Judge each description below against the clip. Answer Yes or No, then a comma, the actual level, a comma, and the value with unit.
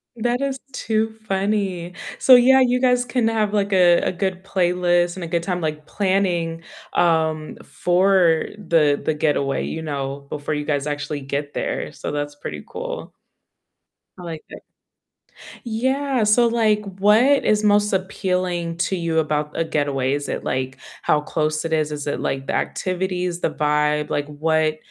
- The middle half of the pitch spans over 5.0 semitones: Yes, wide, 5.4 semitones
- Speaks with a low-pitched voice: No, medium, 175 Hz